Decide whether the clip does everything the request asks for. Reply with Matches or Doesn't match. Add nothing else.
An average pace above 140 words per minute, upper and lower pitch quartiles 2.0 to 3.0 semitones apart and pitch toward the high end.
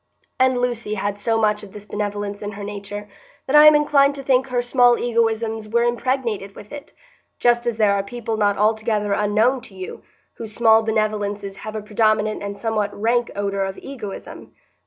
Matches